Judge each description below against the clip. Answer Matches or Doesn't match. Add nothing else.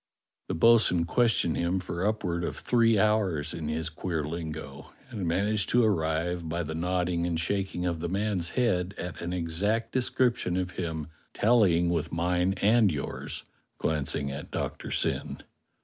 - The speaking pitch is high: Doesn't match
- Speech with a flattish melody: Doesn't match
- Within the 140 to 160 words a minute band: Matches